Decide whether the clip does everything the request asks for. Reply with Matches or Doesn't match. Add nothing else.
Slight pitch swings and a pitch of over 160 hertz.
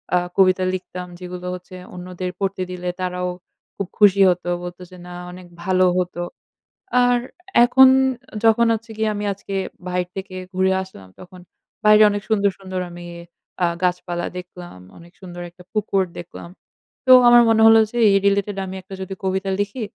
Matches